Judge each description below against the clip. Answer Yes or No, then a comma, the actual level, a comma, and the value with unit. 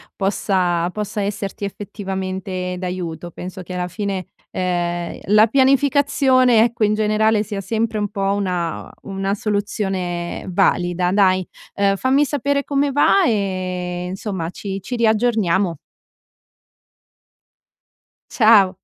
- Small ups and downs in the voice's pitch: No, average, 3.2 semitones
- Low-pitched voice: No, high, 195 Hz